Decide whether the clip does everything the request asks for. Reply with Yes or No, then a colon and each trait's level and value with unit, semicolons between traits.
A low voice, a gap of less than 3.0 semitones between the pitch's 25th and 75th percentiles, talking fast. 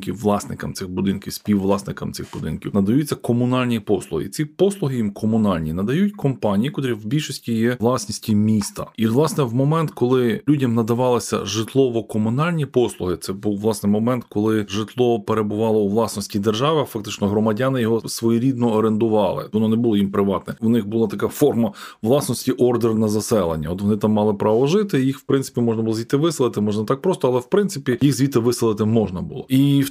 No: low, 115 Hz; average, 3.7 semitones; fast, 170 wpm